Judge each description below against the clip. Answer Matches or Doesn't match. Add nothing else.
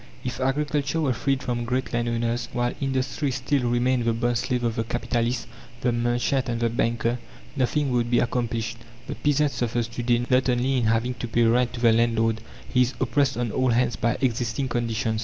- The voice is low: Matches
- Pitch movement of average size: Doesn't match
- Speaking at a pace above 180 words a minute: Matches